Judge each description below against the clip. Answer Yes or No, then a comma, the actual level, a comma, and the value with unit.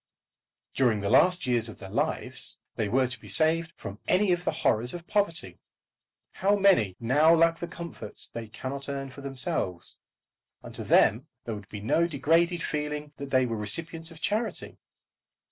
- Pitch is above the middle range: No, medium, 140 Hz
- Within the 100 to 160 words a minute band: No, average, 180 wpm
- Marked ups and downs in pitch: Yes, wide, 6.6 semitones